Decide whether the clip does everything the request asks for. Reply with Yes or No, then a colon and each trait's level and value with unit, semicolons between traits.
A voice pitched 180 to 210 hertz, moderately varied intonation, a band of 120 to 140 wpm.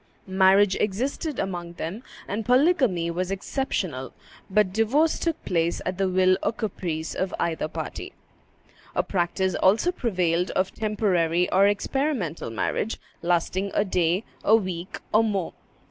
Yes: high, 190 Hz; average, 3.8 semitones; slow, 135 wpm